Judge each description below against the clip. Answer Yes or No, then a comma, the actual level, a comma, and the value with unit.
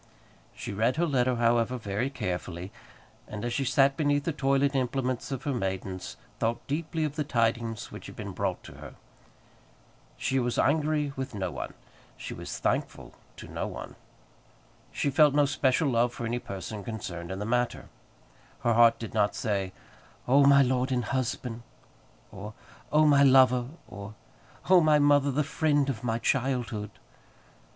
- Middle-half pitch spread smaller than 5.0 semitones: Yes, average, 3.8 semitones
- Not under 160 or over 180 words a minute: Yes, average, 165 wpm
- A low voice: Yes, low, 125 Hz